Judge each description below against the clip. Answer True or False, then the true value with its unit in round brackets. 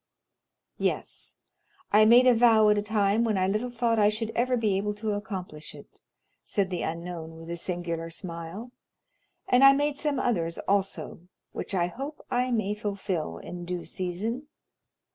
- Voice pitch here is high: True (205 Hz)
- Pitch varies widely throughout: False (4.7 semitones)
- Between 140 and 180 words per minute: True (165 wpm)